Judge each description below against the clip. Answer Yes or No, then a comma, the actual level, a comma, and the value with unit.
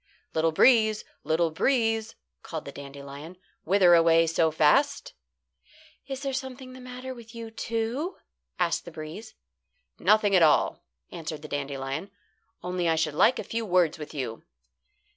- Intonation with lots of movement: Yes, wide, 6.7 semitones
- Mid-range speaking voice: Yes, medium, 180 Hz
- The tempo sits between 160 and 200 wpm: No, average, 145 wpm